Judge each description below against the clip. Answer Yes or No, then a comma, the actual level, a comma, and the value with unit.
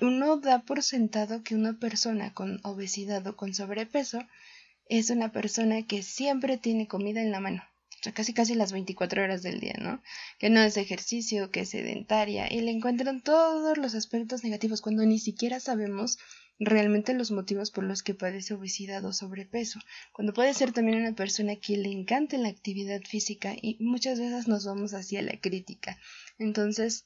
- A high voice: Yes, high, 215 Hz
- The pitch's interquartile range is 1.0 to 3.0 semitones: Yes, average, 2.7 semitones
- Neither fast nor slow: Yes, average, 180 wpm